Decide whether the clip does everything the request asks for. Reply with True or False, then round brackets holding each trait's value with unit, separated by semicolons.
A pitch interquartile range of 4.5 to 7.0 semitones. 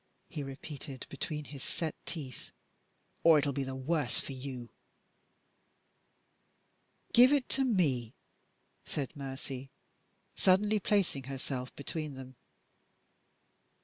False (3.9 semitones)